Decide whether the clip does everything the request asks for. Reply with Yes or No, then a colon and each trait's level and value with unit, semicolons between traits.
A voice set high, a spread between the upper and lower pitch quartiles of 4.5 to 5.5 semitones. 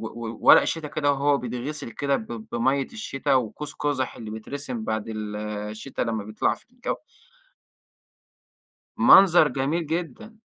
No: low, 135 Hz; average, 5.0 semitones